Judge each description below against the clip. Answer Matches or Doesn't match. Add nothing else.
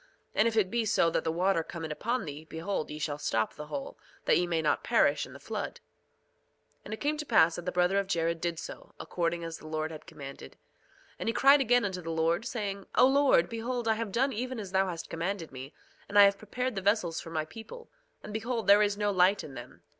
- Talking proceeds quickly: Matches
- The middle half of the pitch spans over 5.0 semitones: Matches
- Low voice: Doesn't match